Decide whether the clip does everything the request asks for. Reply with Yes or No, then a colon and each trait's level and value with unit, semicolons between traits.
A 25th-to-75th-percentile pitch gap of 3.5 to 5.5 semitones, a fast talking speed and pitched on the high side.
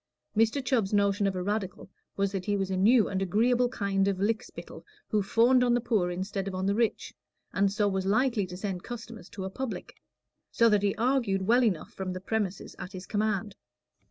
No: average, 3.0 semitones; fast, 215 wpm; high, 205 Hz